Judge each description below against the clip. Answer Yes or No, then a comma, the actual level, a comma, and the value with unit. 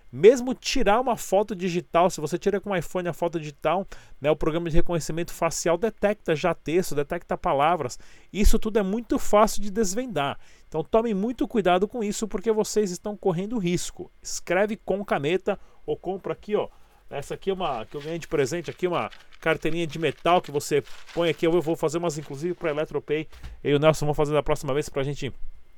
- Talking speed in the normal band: No, fast, 205 wpm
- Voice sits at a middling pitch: Yes, medium, 175 Hz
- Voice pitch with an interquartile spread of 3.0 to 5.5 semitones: Yes, average, 4.7 semitones